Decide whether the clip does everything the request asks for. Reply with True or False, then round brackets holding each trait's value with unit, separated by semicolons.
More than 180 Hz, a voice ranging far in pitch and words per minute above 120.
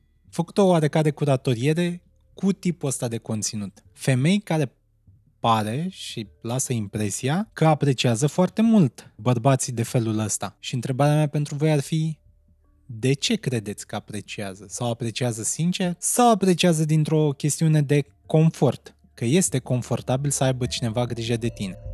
False (130 Hz; 5.8 semitones; 145 wpm)